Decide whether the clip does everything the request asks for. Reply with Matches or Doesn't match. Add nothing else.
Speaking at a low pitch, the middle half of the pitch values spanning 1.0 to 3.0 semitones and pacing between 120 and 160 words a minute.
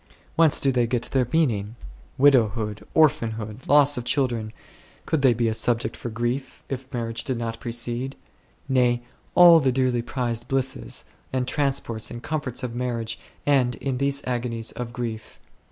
Matches